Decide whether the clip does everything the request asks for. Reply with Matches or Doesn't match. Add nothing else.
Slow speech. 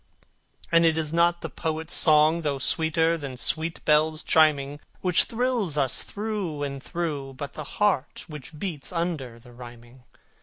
Doesn't match